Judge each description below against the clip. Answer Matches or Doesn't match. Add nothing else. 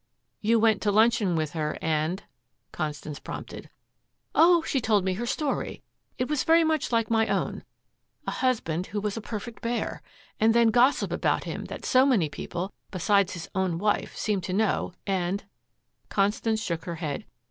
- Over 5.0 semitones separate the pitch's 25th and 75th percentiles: Doesn't match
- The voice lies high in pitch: Matches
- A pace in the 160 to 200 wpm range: Matches